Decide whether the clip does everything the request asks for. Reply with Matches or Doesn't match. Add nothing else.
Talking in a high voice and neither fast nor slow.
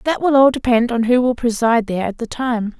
Doesn't match